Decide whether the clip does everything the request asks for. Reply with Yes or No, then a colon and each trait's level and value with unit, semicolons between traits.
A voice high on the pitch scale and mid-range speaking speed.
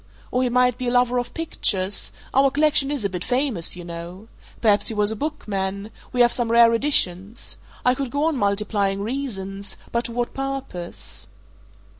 Yes: high, 230 Hz; average, 180 wpm